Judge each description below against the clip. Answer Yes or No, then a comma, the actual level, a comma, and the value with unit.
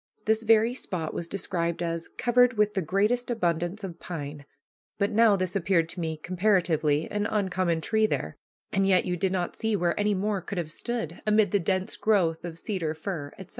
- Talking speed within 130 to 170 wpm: No, average, 195 wpm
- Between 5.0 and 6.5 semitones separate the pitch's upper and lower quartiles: No, average, 3.9 semitones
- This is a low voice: No, medium, 185 Hz